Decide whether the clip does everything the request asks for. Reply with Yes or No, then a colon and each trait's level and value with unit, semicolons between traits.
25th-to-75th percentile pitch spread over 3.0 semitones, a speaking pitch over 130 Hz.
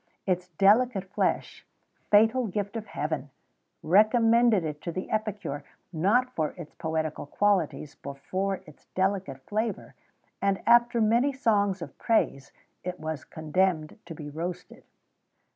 Yes: wide, 5.4 semitones; high, 190 Hz